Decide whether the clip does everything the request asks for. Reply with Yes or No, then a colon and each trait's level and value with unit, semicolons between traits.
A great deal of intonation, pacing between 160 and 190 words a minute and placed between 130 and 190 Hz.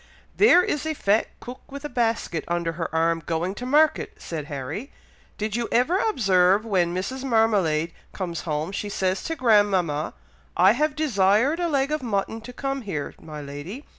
No: wide, 7.4 semitones; average, 175 wpm; high, 205 Hz